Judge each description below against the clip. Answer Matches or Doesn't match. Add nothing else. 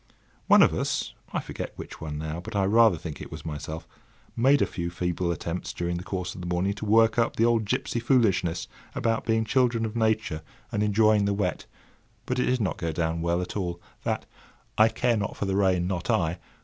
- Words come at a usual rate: Doesn't match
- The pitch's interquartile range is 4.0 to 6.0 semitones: Matches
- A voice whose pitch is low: Matches